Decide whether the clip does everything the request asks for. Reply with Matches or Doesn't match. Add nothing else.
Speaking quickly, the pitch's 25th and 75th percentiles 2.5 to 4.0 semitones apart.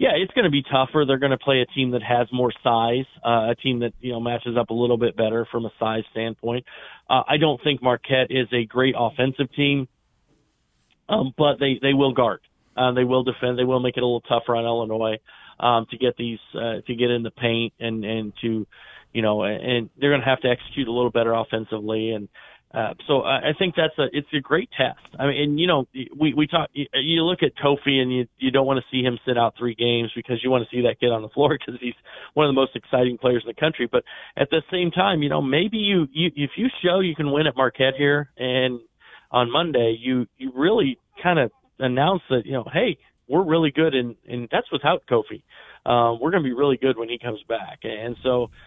Matches